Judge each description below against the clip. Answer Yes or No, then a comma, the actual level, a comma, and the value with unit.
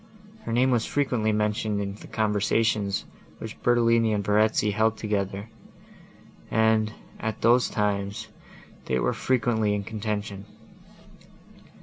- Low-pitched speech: Yes, low, 110 Hz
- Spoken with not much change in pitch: Yes, narrow, 1.6 semitones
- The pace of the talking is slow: Yes, slow, 115 wpm